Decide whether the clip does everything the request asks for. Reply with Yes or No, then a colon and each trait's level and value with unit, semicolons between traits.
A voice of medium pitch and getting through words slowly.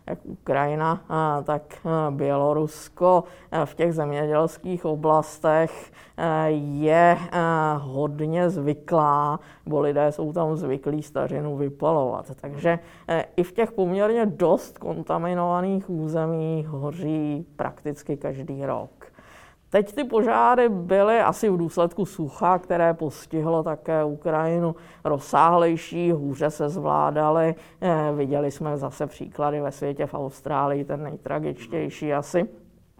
Yes: medium, 155 Hz; slow, 105 wpm